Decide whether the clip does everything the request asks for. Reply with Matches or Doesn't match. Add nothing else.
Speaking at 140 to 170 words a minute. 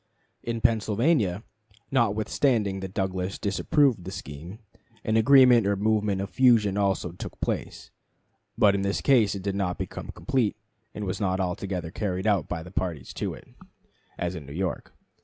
Matches